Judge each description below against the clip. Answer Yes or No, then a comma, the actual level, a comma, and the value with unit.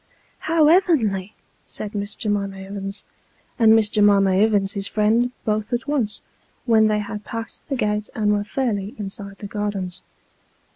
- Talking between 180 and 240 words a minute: No, average, 155 wpm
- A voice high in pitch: Yes, high, 210 Hz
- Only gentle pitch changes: Yes, narrow, 1.9 semitones